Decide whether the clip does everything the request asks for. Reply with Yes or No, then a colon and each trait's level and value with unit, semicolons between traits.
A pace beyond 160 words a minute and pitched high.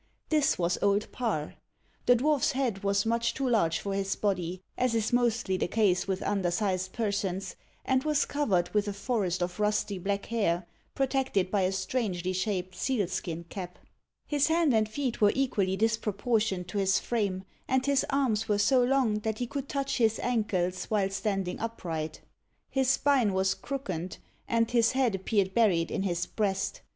Yes: average, 170 wpm; high, 210 Hz